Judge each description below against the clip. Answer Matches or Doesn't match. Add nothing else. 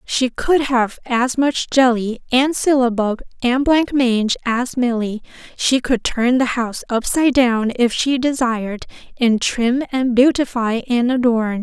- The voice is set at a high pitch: Matches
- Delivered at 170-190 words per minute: Doesn't match